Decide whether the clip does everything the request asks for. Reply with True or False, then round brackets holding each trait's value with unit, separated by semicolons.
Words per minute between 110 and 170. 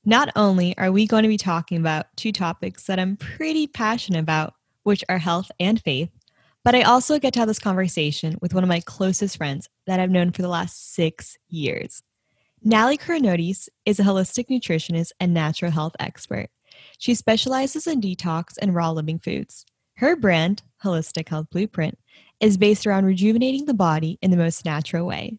False (180 wpm)